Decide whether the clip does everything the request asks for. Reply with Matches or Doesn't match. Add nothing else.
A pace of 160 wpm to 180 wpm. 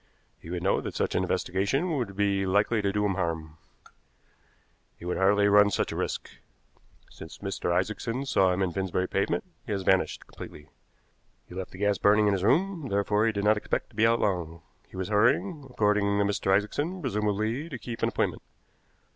Doesn't match